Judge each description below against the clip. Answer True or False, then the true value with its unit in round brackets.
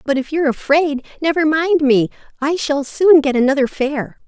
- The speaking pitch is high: True (290 Hz)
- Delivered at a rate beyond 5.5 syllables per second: False (5.0 syllables/s)